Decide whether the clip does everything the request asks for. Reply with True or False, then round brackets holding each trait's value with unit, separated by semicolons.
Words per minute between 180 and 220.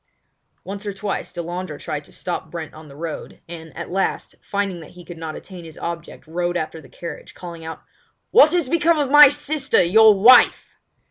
True (195 wpm)